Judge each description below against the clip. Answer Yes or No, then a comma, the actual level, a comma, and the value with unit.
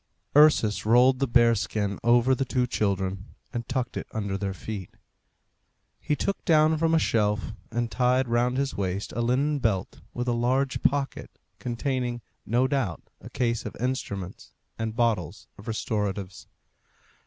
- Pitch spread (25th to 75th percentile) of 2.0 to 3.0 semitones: No, average, 3.9 semitones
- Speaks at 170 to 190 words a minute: No, average, 155 wpm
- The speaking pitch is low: Yes, low, 120 Hz